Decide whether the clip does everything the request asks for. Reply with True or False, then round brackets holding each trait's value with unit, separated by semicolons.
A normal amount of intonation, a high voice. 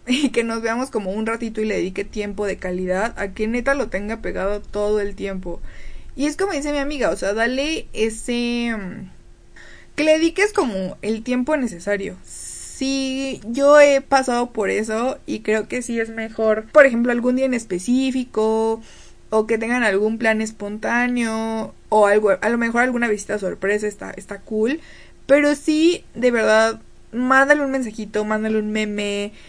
True (3.6 semitones; 225 Hz)